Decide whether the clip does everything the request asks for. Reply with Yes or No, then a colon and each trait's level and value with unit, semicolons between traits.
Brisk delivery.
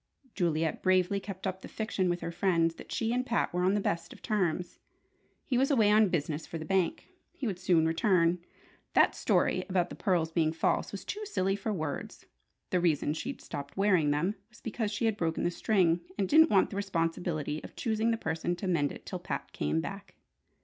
Yes: fast, 210 wpm